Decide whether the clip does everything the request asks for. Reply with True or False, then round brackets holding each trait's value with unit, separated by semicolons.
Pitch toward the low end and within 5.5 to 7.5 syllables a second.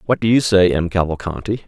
True (100 Hz; 6.0 syllables/s)